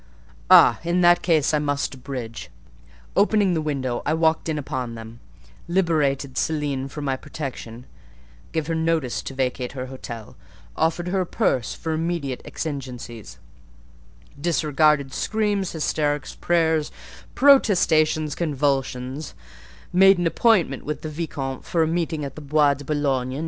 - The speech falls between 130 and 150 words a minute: Yes, average, 140 wpm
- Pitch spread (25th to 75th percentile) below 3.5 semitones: No, average, 3.8 semitones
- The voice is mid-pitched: Yes, medium, 150 Hz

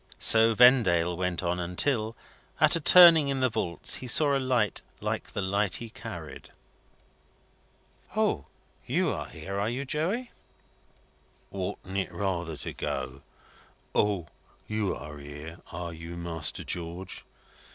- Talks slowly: Yes, slow, 130 wpm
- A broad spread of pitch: Yes, wide, 6.5 semitones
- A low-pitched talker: Yes, very low, 95 Hz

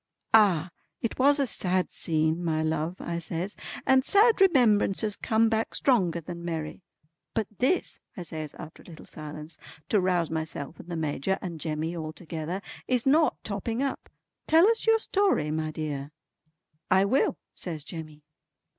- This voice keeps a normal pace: Yes, average, 160 wpm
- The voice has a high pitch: No, medium, 175 Hz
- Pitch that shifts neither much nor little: No, wide, 6.2 semitones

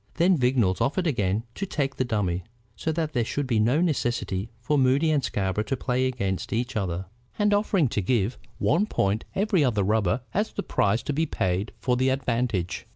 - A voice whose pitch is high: No, low, 125 Hz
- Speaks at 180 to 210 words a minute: Yes, average, 195 wpm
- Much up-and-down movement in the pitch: Yes, wide, 6.4 semitones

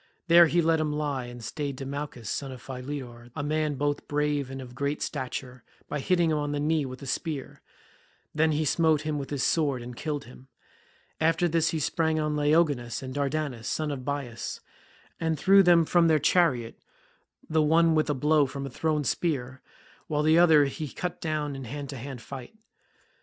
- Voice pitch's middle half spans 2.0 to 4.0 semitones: Yes, average, 2.8 semitones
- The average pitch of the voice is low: No, medium, 145 Hz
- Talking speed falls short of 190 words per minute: No, average, 195 wpm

